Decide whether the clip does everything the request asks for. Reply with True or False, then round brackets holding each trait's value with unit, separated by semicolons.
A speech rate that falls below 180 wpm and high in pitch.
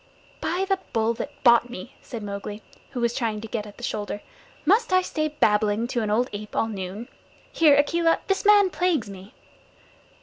False (190 wpm; 235 Hz)